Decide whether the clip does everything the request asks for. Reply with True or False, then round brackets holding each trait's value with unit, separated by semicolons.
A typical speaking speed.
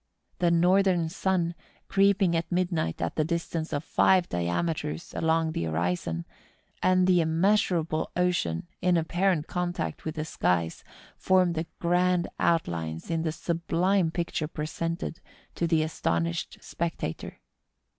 False (125 wpm)